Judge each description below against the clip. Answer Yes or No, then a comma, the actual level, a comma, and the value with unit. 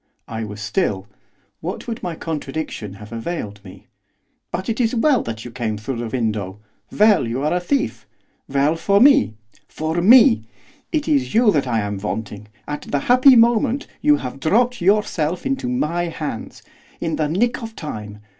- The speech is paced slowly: No, average, 175 wpm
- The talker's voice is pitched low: No, medium, 160 Hz